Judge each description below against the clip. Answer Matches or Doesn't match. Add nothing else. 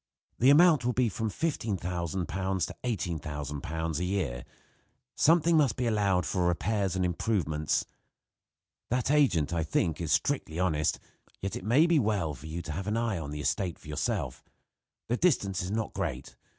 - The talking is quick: Doesn't match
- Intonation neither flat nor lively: Doesn't match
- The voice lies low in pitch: Matches